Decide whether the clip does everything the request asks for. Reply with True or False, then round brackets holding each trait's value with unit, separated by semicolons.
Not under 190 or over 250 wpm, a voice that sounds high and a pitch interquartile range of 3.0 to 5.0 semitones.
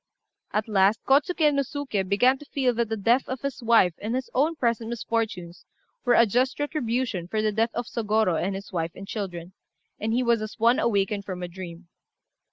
True (200 wpm; 225 Hz; 4.3 semitones)